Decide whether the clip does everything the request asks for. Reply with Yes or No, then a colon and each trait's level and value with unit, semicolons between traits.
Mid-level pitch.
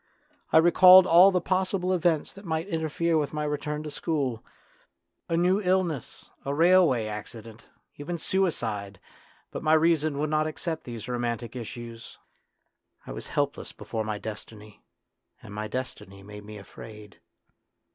Yes: medium, 150 Hz